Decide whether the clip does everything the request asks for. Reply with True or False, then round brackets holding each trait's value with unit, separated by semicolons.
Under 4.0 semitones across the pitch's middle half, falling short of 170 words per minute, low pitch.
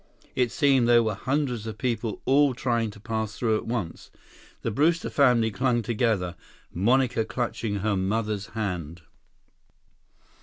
True (3.0 semitones; 140 wpm; 115 Hz)